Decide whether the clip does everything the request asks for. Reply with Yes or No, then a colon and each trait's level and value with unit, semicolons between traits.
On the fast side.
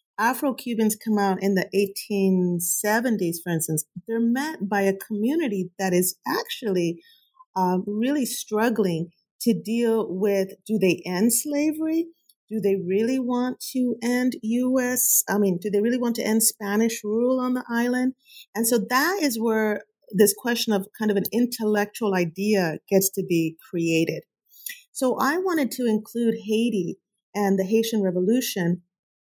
No: average, 150 wpm